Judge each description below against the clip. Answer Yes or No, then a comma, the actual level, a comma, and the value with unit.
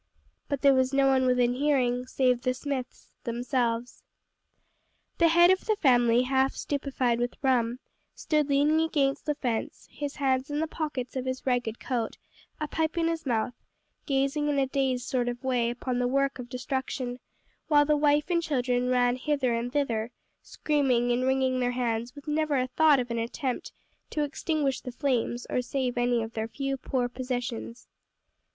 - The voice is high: Yes, very high, 260 Hz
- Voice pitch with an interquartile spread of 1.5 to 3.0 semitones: Yes, average, 2.7 semitones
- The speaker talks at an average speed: Yes, average, 175 wpm